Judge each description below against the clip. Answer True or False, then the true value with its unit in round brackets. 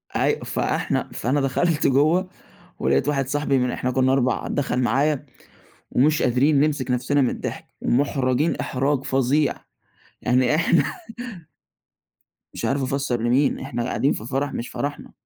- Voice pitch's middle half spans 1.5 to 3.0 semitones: True (2.5 semitones)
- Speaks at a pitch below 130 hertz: False (135 Hz)